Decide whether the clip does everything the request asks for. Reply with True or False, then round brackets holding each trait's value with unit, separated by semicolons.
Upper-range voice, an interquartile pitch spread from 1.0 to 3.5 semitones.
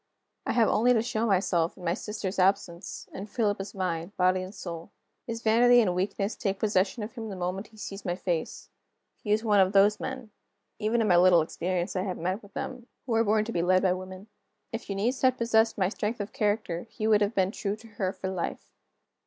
True (200 Hz; 3.1 semitones)